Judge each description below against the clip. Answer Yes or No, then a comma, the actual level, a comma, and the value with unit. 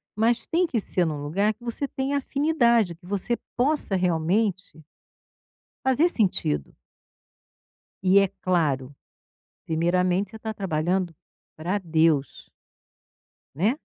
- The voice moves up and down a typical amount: No, wide, 6.0 semitones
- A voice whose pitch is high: Yes, high, 195 Hz